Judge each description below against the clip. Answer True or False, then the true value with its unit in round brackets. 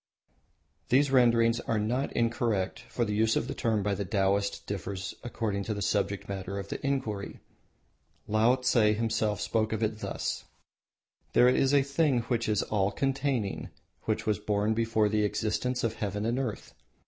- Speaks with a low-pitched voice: True (110 Hz)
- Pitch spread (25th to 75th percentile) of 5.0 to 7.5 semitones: False (2.7 semitones)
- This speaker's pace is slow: False (165 wpm)